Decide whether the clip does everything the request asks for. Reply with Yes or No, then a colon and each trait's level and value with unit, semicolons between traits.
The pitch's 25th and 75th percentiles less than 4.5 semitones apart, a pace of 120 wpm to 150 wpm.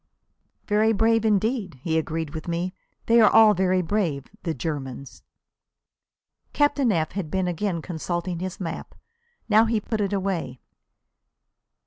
No: average, 4.8 semitones; slow, 135 wpm